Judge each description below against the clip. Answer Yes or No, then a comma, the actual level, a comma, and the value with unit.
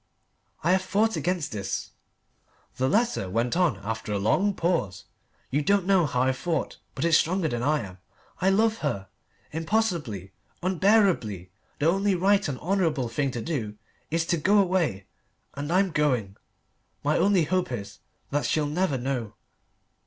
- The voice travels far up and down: Yes, wide, 7.5 semitones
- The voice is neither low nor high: Yes, medium, 155 Hz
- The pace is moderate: Yes, average, 160 wpm